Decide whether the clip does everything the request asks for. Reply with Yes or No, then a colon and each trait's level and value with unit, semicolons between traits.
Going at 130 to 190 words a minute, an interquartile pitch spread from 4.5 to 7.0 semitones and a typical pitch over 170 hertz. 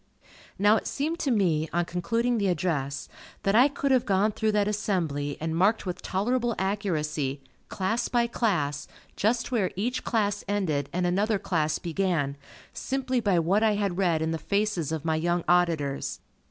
Yes: average, 170 wpm; average, 5.1 semitones; high, 190 Hz